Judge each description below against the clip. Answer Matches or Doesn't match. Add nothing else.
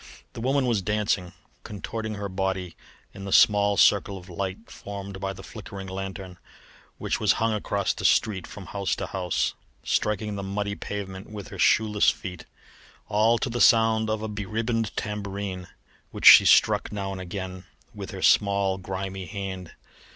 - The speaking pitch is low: Matches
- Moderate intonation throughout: Doesn't match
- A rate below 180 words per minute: Matches